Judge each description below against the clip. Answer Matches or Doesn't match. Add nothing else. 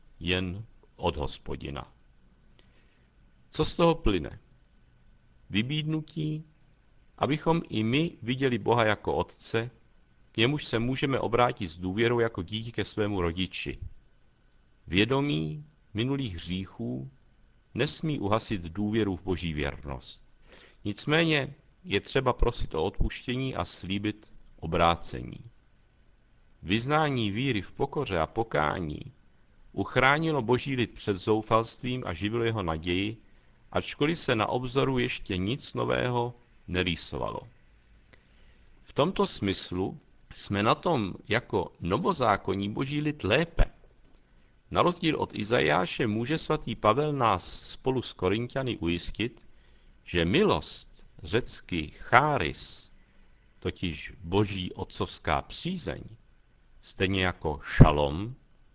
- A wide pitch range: Matches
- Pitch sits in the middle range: Doesn't match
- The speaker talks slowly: Matches